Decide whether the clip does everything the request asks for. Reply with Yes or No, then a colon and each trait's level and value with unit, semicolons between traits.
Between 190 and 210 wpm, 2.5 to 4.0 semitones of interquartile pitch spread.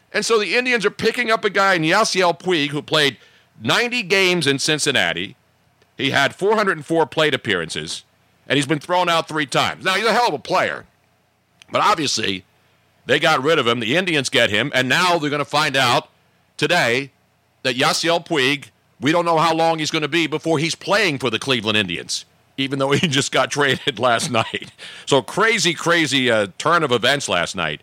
No: average, 200 wpm; average, 4.4 semitones